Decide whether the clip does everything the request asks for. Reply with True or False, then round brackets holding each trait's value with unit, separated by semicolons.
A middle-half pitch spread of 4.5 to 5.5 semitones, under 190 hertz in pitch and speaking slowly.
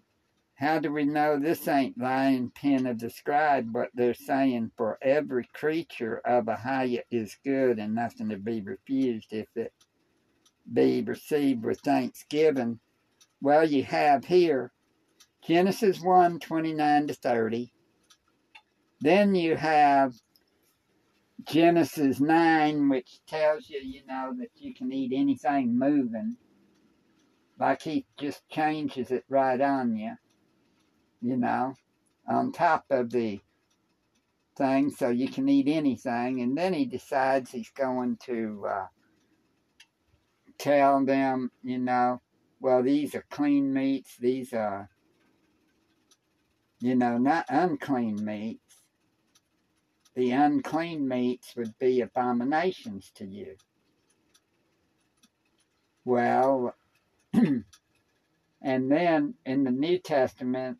True (5.2 semitones; 135 Hz; 115 wpm)